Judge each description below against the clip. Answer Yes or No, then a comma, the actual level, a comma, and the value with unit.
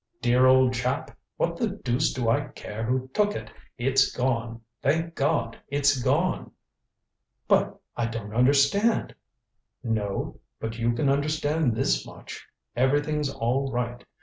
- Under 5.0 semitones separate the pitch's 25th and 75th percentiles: Yes, average, 3.6 semitones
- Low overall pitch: Yes, low, 130 Hz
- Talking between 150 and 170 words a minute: No, average, 140 wpm